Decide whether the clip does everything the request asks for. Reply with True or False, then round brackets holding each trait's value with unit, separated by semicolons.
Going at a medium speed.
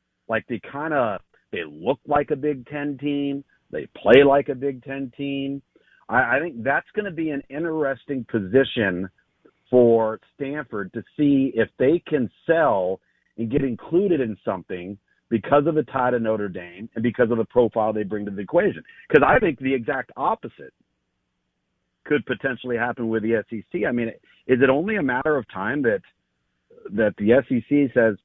True (180 wpm)